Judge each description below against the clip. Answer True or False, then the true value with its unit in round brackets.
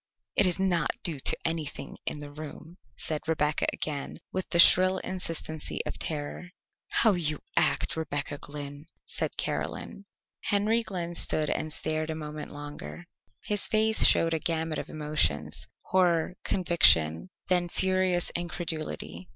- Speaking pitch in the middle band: True (160 Hz)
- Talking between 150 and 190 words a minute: False (140 wpm)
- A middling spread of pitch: True (3.4 semitones)